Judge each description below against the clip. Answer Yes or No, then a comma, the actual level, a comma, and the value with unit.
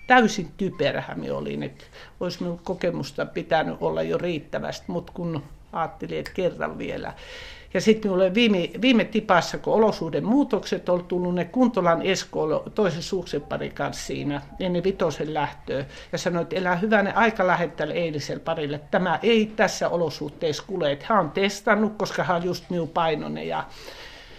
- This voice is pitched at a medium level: Yes, medium, 180 Hz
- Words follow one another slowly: No, fast, 155 wpm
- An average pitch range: Yes, average, 3.9 semitones